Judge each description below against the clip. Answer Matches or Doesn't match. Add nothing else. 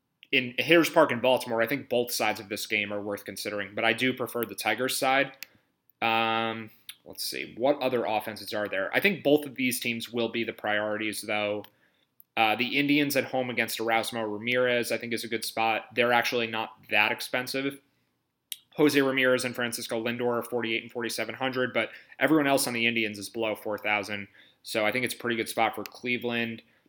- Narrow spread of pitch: Matches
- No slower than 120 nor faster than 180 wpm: Doesn't match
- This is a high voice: Doesn't match